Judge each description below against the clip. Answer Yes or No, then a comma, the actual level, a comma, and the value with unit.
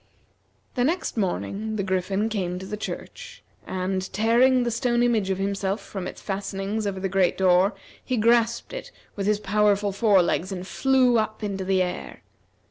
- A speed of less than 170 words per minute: No, average, 175 wpm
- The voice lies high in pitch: Yes, high, 200 Hz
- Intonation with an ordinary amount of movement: Yes, average, 3.0 semitones